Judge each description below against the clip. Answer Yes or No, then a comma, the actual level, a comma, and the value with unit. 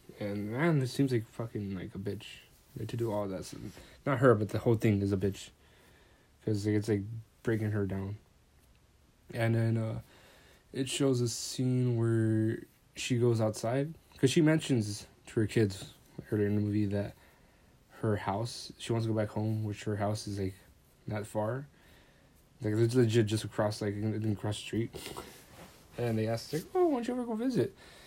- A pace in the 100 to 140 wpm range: No, average, 185 wpm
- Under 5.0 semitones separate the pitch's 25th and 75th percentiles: Yes, average, 3.0 semitones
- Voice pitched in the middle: No, low, 110 Hz